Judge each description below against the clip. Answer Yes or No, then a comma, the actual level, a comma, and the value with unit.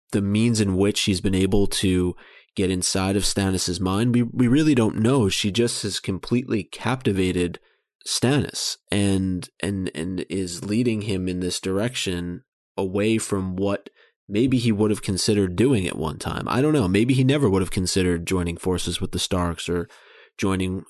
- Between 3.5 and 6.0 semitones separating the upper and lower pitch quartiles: No, average, 3.0 semitones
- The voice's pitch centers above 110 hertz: No, very low, 95 Hz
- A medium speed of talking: Yes, average, 175 wpm